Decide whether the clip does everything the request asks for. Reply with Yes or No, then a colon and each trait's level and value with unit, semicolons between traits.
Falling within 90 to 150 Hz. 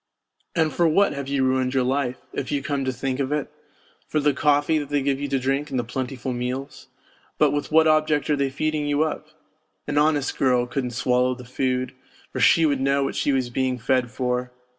Yes: low, 135 Hz